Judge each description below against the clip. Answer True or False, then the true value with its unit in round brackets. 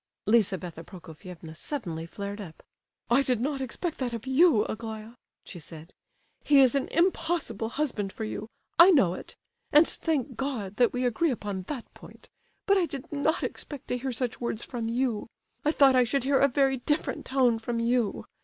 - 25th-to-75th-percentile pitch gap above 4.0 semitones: True (4.7 semitones)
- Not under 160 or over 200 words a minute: True (180 wpm)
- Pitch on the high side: True (245 Hz)